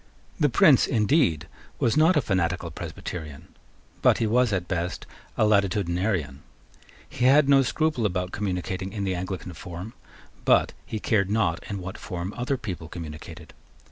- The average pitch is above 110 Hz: No, very low, 95 Hz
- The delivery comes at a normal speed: Yes, average, 150 wpm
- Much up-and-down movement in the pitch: No, average, 4.2 semitones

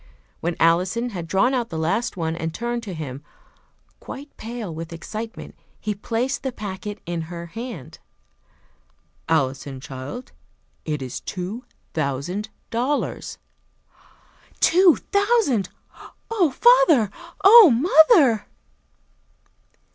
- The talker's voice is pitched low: No, high, 210 Hz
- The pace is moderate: No, slow, 110 wpm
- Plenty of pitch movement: Yes, wide, 7.6 semitones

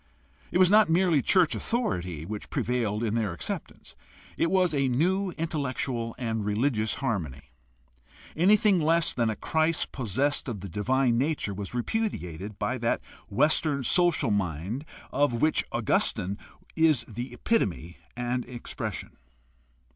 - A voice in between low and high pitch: No, low, 125 Hz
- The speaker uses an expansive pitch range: Yes, wide, 7.2 semitones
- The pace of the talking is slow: Yes, slow, 130 wpm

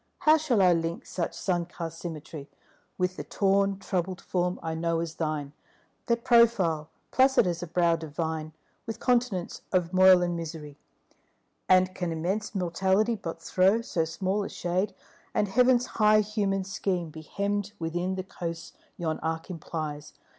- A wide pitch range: No, average, 3.4 semitones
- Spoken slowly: No, average, 155 wpm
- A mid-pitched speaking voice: Yes, medium, 180 Hz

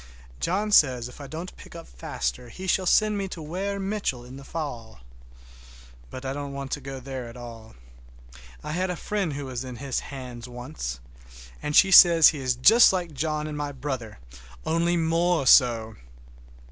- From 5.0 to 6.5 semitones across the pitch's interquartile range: Yes, wide, 5.5 semitones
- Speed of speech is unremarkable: Yes, average, 185 wpm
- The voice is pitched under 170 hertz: Yes, medium, 140 Hz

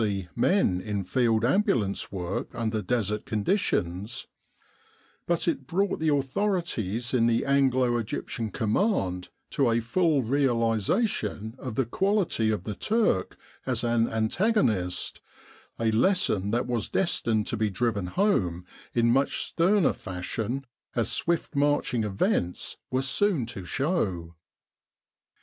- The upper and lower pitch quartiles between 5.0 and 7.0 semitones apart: Yes, wide, 5.5 semitones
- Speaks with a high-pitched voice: No, low, 115 Hz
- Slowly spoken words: Yes, slow, 125 wpm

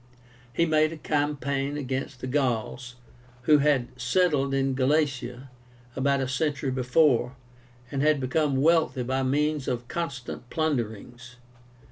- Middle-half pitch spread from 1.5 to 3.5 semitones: Yes, average, 2.9 semitones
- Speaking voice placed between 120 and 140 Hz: Yes, low, 135 Hz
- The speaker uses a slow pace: Yes, slow, 125 wpm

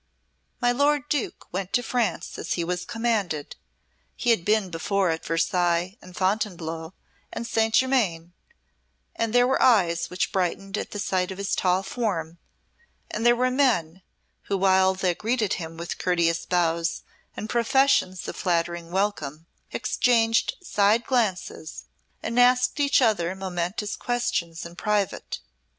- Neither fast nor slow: Yes, average, 145 wpm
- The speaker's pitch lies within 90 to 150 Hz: No, high, 195 Hz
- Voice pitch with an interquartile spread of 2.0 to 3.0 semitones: No, average, 5.2 semitones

